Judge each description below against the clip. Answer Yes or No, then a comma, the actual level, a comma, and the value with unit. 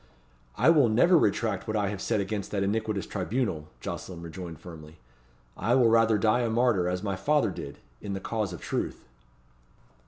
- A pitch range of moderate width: Yes, average, 3.9 semitones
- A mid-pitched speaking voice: No, low, 105 Hz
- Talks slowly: No, average, 180 wpm